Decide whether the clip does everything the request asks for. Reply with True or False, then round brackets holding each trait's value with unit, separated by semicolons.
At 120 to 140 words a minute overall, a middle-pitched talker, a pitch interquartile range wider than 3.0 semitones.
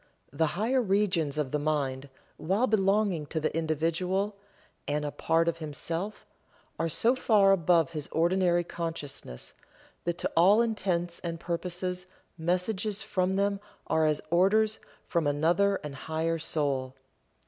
True (135 wpm; 170 Hz; 3.7 semitones)